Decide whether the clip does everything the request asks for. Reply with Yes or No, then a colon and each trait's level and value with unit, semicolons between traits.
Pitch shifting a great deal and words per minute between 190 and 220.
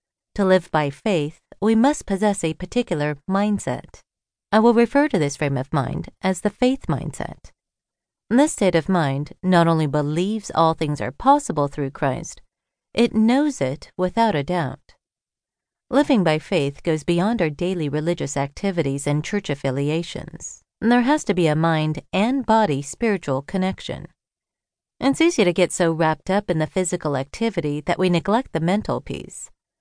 No: wide, 6.0 semitones; average, 160 wpm